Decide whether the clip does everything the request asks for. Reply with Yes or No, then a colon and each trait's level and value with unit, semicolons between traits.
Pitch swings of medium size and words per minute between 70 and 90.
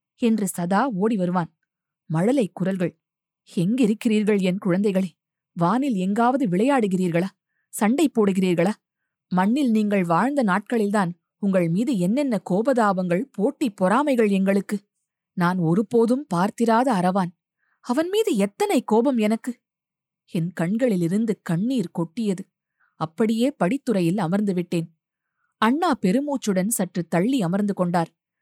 No: average, 4.6 semitones; average, 100 wpm